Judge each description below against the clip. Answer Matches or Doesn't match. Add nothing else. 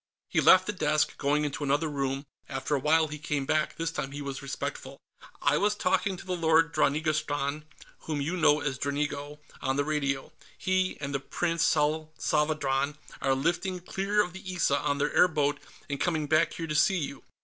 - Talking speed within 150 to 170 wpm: Doesn't match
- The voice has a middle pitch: Matches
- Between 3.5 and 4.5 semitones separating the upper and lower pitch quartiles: Doesn't match